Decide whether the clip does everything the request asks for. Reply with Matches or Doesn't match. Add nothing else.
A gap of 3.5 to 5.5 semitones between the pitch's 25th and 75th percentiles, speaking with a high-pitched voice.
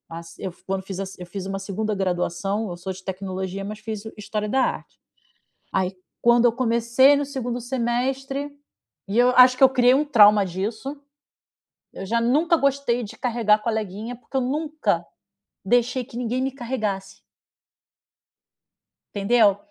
Matches